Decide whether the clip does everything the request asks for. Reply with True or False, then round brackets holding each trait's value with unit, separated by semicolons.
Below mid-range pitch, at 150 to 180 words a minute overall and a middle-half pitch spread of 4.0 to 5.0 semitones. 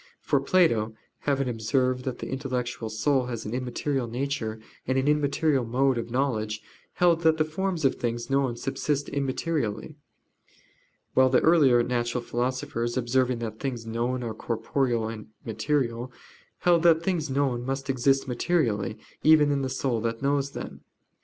False (130 Hz; 155 wpm; 3.2 semitones)